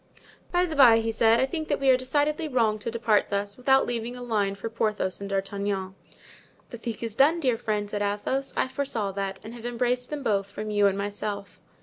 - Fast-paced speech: Yes, fast, 220 wpm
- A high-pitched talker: Yes, high, 225 Hz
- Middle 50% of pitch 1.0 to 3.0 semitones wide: No, average, 4.1 semitones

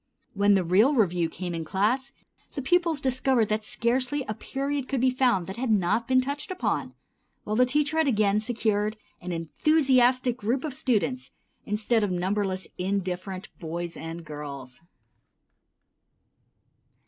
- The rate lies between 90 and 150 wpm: Yes, average, 145 wpm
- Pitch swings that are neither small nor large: No, wide, 5.8 semitones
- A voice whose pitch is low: No, high, 215 Hz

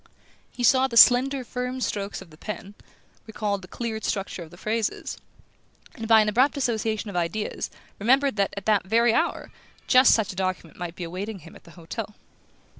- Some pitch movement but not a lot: Yes, average, 4.2 semitones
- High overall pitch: Yes, high, 215 Hz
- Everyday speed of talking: Yes, average, 190 wpm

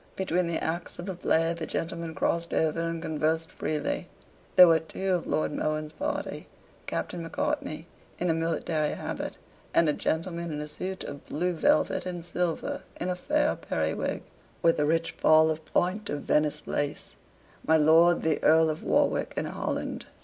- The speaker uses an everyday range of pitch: No, narrow, 2.0 semitones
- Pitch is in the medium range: Yes, medium, 165 Hz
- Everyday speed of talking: Yes, average, 170 wpm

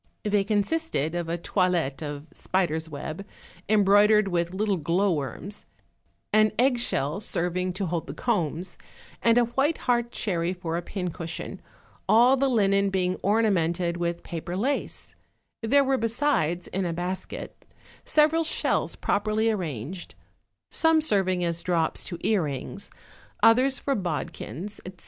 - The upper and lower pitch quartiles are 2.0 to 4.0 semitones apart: No, average, 4.5 semitones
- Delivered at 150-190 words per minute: No, slow, 135 wpm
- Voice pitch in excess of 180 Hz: Yes, high, 190 Hz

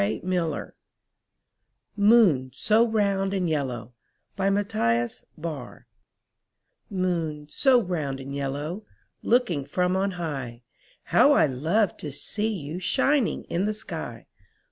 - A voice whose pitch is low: No, medium, 180 Hz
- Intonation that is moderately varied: No, wide, 6.8 semitones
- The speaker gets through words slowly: Yes, slow, 105 wpm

